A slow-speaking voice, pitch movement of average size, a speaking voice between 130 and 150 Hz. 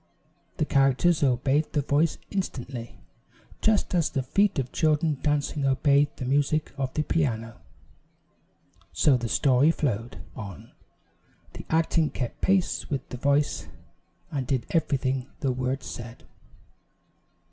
Yes: slow, 125 wpm; average, 3.1 semitones; medium, 140 Hz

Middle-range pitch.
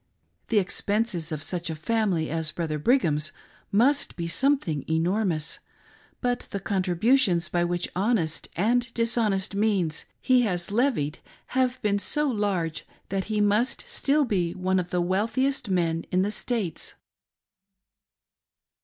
No: high, 195 Hz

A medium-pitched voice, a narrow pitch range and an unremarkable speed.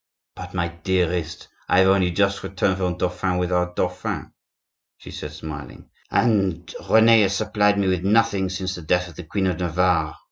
No: very low, 90 Hz; narrow, 1.8 semitones; average, 180 wpm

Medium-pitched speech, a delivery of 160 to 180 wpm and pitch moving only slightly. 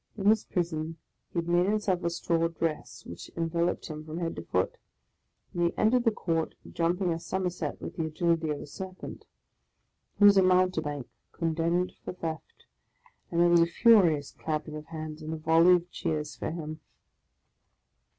Yes: medium, 170 Hz; average, 175 wpm; narrow, 2.3 semitones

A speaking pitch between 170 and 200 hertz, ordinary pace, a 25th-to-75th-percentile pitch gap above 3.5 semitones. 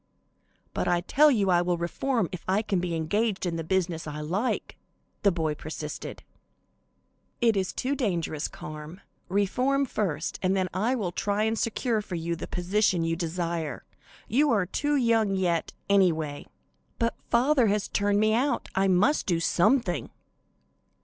Yes: high, 190 Hz; average, 160 wpm; average, 4.8 semitones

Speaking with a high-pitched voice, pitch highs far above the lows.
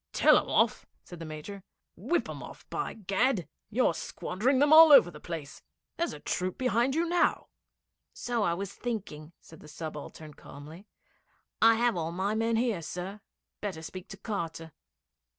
Yes: high, 195 Hz; wide, 6.3 semitones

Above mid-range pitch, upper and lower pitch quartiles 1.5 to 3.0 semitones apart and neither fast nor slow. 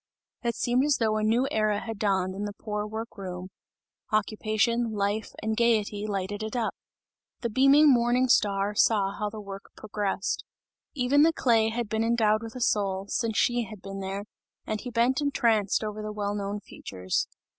Yes: high, 215 Hz; narrow, 2.5 semitones; average, 180 wpm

